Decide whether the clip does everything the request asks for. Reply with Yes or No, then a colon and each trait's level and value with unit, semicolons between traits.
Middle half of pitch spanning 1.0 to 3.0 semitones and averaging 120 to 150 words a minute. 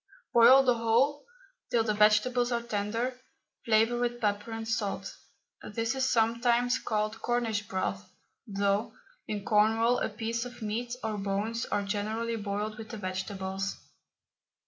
Yes: narrow, 2.5 semitones; average, 140 wpm